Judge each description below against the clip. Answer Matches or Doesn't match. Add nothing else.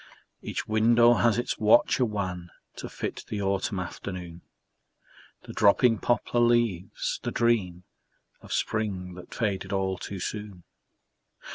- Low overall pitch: Matches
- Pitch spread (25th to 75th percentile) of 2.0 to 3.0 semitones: Doesn't match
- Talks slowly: Matches